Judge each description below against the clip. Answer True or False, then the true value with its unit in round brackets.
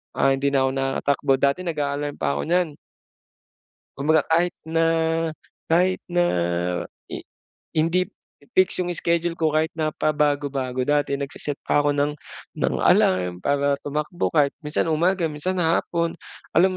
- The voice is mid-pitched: True (150 Hz)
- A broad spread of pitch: False (3.0 semitones)